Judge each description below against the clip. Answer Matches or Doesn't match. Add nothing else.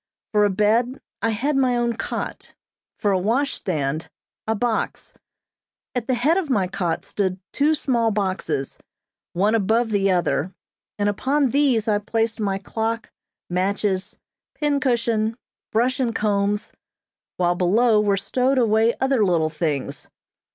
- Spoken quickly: Doesn't match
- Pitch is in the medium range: Doesn't match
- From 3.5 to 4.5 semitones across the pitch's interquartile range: Matches